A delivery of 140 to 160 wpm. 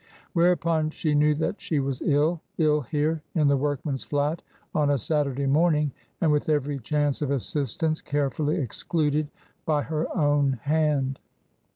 Yes: average, 155 wpm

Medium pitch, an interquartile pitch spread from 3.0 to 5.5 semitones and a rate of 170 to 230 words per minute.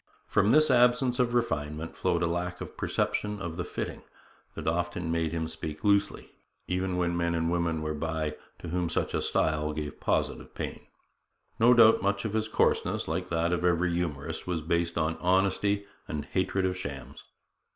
No: very low, 85 Hz; average, 3.4 semitones; average, 180 wpm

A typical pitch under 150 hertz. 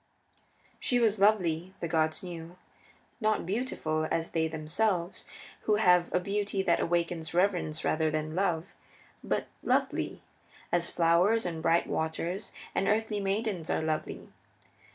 No: medium, 175 Hz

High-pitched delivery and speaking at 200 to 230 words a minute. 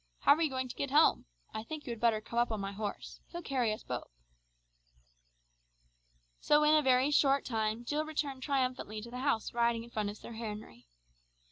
Yes: high, 240 Hz; fast, 205 wpm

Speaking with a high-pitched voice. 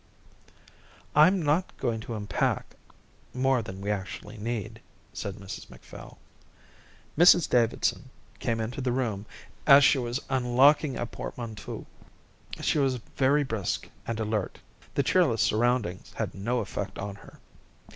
No: low, 120 Hz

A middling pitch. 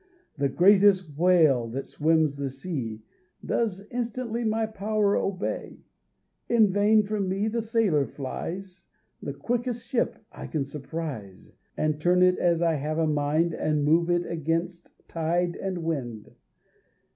Yes: medium, 170 Hz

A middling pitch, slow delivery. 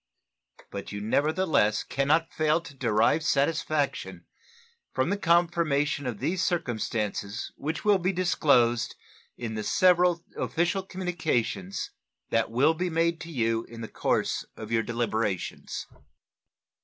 Yes: medium, 145 Hz; slow, 130 wpm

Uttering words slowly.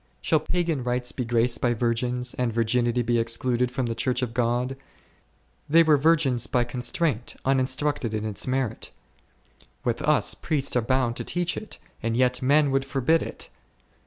No: average, 165 wpm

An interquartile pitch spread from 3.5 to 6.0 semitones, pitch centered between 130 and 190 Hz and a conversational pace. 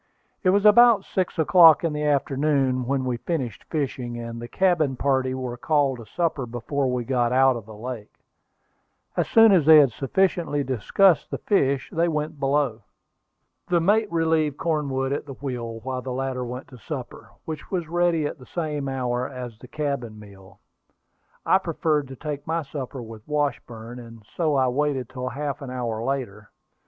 Yes: average, 3.9 semitones; low, 135 Hz; average, 180 wpm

